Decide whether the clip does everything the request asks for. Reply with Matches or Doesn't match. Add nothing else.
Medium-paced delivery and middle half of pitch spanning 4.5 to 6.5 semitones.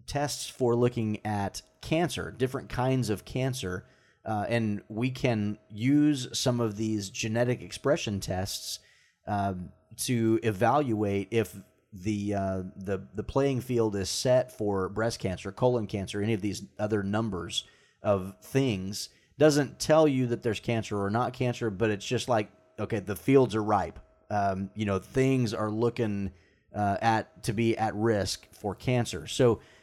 Doesn't match